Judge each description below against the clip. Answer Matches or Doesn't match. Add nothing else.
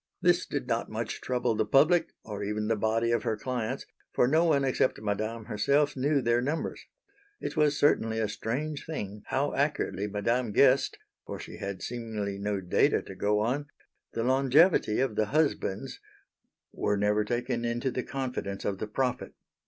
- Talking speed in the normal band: Matches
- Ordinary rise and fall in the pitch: Matches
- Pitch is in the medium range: Doesn't match